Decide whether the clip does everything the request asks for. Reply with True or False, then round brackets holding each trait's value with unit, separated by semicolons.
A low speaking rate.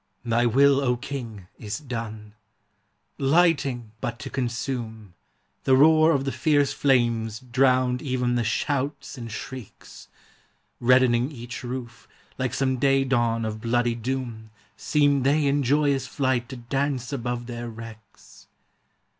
True (130 wpm)